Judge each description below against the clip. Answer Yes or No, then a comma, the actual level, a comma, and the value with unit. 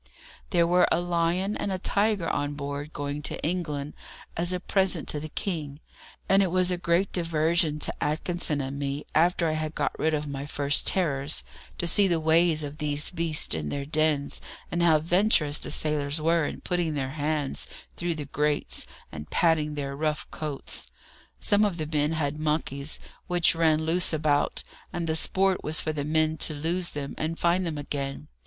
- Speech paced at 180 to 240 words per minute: Yes, average, 190 wpm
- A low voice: No, medium, 155 Hz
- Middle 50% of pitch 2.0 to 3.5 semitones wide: Yes, average, 2.8 semitones